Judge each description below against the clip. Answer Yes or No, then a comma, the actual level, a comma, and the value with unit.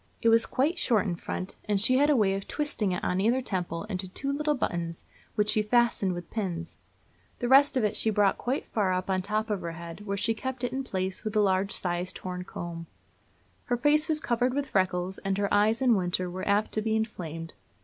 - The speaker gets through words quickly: Yes, fast, 230 wpm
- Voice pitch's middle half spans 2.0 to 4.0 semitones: No, average, 4.7 semitones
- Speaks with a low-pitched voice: No, high, 205 Hz